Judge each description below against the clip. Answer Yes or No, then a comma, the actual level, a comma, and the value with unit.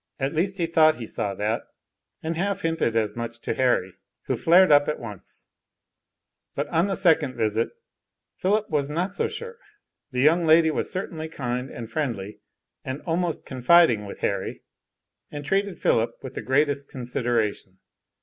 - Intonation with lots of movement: Yes, wide, 5.9 semitones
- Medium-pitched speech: Yes, medium, 145 Hz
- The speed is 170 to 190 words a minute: No, average, 160 wpm